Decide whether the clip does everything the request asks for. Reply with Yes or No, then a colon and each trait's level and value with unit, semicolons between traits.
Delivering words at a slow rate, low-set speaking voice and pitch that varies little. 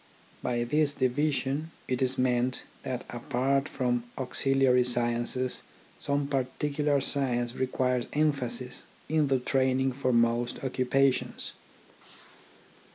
Yes: slow, 110 wpm; low, 130 Hz; narrow, 1.8 semitones